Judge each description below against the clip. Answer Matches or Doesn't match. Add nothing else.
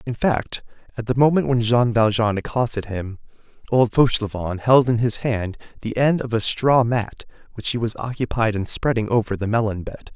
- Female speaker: Doesn't match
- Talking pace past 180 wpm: Matches